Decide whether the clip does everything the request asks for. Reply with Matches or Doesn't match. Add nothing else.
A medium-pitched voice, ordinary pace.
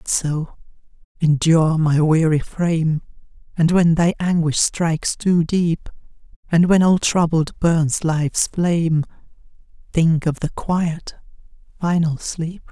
Doesn't match